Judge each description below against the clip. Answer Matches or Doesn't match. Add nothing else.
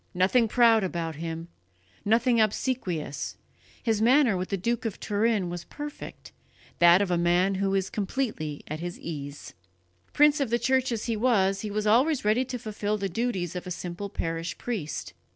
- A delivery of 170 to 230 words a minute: Matches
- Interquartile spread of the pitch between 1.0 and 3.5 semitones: Doesn't match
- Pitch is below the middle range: Doesn't match